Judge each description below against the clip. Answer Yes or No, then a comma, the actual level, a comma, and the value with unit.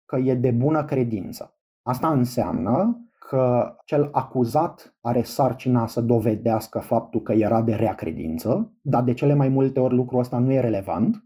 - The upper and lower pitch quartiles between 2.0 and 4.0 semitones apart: Yes, narrow, 2.6 semitones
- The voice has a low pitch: Yes, low, 125 Hz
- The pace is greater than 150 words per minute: Yes, average, 165 wpm